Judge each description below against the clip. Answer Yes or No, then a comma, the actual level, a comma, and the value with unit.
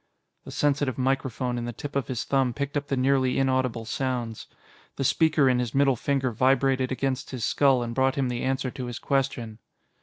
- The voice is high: No, low, 130 Hz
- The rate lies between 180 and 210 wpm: Yes, average, 195 wpm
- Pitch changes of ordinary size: No, narrow, 1.8 semitones